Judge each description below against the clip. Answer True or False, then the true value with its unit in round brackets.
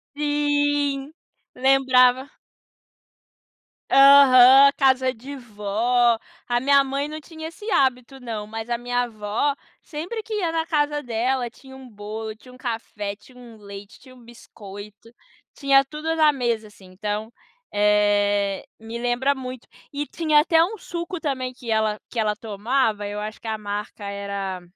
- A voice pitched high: True (245 Hz)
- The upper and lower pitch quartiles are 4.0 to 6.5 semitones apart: True (4.6 semitones)